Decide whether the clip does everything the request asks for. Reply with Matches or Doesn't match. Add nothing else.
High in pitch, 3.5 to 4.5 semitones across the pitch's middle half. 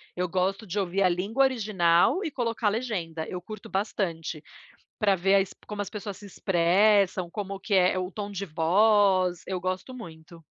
Doesn't match